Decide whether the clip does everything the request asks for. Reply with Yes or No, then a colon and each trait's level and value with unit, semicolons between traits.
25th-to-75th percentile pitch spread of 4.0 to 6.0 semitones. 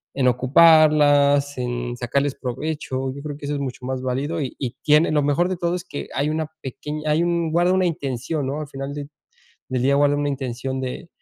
No: average, 2.7 semitones